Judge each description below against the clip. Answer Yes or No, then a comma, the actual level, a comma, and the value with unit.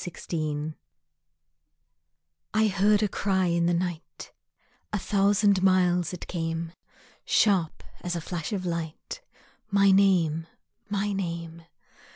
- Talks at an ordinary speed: No, slow, 115 wpm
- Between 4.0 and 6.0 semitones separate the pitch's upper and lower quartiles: No, average, 2.9 semitones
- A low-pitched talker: No, medium, 180 Hz